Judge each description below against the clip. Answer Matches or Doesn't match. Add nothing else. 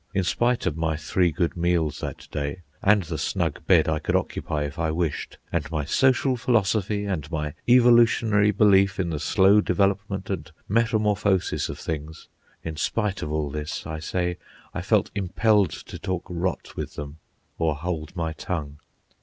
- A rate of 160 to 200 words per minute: Matches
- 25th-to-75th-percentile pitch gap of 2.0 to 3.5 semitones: Doesn't match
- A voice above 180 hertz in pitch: Doesn't match